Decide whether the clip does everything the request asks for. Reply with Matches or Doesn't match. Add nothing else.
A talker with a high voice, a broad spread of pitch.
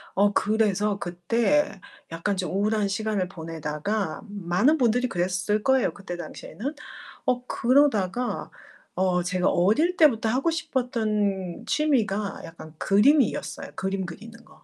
Doesn't match